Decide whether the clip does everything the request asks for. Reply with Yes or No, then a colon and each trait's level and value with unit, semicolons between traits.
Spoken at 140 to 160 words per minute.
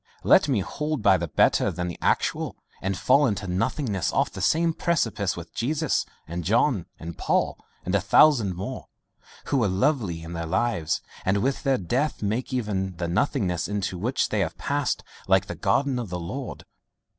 No: average, 180 wpm